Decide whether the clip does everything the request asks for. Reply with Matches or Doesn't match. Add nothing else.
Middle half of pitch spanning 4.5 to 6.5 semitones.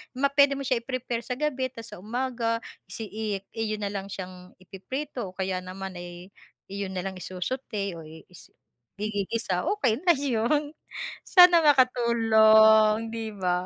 Matches